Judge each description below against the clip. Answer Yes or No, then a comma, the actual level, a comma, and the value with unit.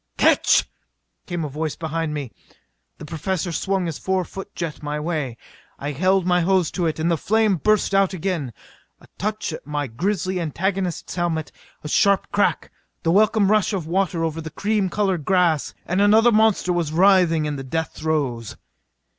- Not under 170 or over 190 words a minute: Yes, average, 175 wpm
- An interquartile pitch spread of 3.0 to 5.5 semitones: Yes, average, 3.8 semitones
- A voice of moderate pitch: Yes, medium, 175 Hz